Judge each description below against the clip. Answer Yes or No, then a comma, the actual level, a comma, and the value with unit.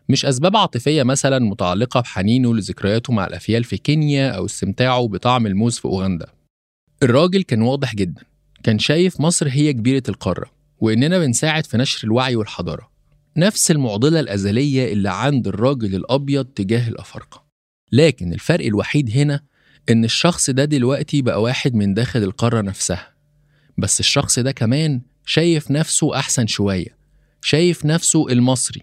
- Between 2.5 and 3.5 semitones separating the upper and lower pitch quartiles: No, average, 4.9 semitones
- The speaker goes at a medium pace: No, fast, 140 wpm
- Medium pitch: No, low, 130 Hz